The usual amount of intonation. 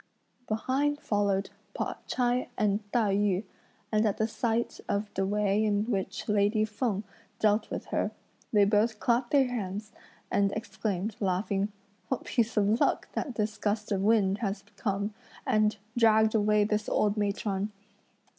No: narrow, 1.7 semitones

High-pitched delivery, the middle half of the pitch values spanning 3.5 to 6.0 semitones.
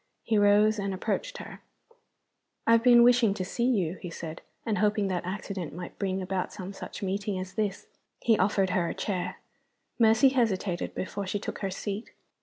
No: high, 200 Hz; average, 2.8 semitones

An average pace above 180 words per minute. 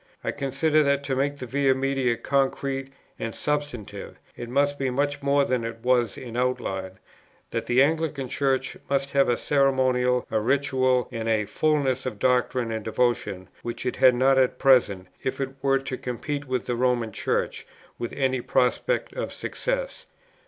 No: average, 170 wpm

